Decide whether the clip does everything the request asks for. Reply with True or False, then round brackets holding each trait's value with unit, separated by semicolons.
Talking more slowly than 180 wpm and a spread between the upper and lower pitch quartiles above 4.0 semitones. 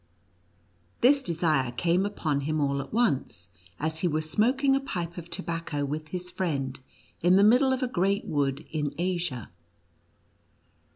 True (155 wpm; 5.3 semitones)